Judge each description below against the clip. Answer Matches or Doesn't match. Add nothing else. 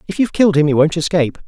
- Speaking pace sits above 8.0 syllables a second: Matches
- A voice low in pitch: Doesn't match